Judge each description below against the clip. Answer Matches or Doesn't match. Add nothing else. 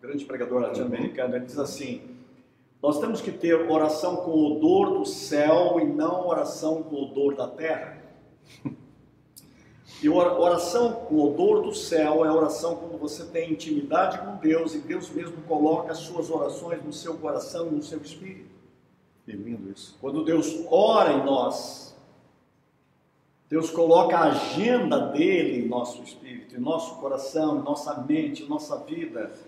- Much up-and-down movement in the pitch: Doesn't match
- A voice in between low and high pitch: Matches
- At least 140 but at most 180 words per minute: Matches